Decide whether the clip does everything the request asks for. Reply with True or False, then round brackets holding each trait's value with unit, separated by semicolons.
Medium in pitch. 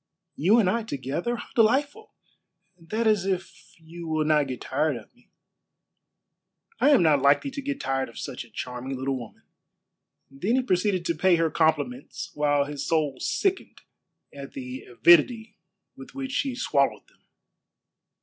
True (165 Hz)